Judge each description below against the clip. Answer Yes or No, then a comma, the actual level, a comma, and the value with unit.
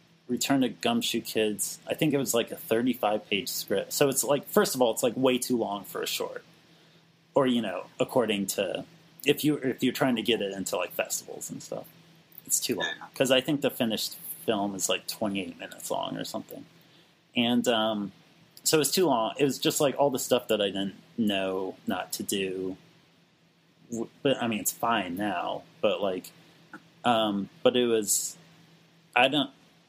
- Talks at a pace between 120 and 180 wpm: No, average, 190 wpm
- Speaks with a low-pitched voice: Yes, low, 125 Hz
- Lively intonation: Yes, wide, 6.3 semitones